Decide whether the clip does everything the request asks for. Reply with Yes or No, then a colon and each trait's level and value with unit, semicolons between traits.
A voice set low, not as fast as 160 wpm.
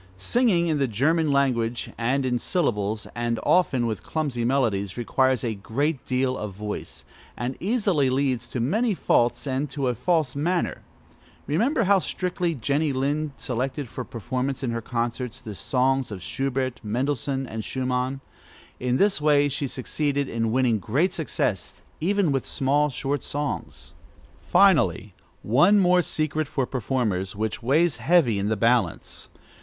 Yes: low, 130 Hz; average, 150 wpm